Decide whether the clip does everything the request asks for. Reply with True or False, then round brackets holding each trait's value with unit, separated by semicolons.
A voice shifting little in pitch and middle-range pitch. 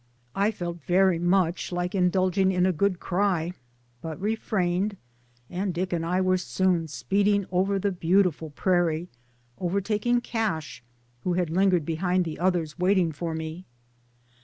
True (2.3 semitones; 180 Hz)